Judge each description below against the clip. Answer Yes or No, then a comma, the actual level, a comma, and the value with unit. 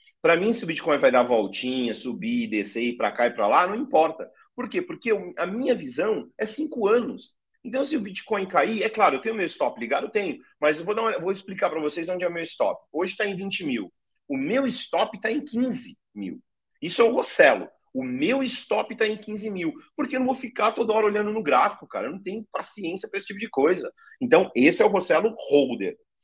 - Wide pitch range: Yes, wide, 5.8 semitones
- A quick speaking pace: Yes, fast, 240 wpm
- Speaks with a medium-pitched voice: No, high, 225 Hz